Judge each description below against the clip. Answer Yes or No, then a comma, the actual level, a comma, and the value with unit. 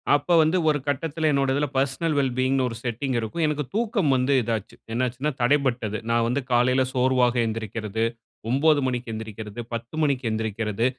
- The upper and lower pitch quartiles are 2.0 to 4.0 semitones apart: Yes, average, 3.7 semitones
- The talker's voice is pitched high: No, low, 130 Hz